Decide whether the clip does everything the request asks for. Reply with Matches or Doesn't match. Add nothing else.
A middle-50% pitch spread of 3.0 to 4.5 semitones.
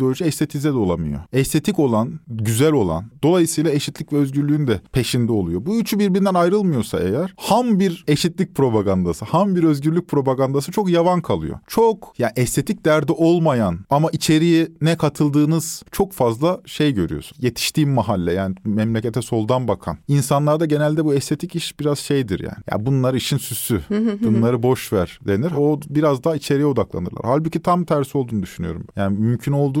Doesn't match